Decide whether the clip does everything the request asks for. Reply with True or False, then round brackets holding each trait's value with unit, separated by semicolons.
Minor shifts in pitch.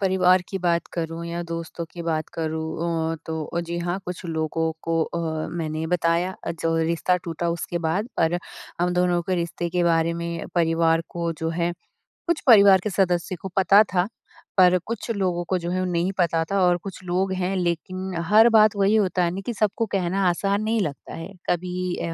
True (2.1 semitones)